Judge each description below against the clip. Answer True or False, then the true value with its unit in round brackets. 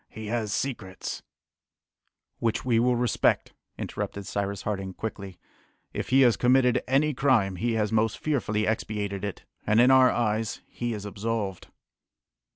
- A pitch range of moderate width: True (3.2 semitones)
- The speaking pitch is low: True (110 Hz)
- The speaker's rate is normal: True (150 wpm)